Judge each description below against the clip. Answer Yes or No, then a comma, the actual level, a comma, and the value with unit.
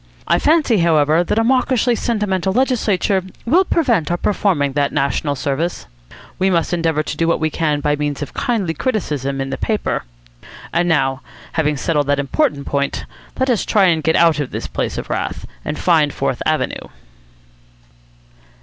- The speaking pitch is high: No, medium, 165 Hz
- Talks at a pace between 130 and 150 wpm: No, average, 170 wpm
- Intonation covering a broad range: Yes, wide, 6.4 semitones